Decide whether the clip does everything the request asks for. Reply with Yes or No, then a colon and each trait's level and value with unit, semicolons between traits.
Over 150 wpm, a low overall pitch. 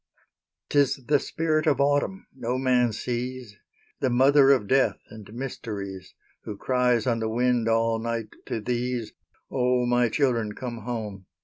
No: average, 145 wpm; low, 120 Hz